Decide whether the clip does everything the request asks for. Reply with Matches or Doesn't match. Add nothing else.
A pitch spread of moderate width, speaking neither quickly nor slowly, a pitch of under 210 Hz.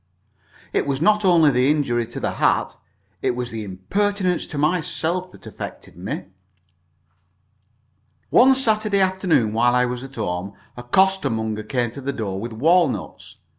Doesn't match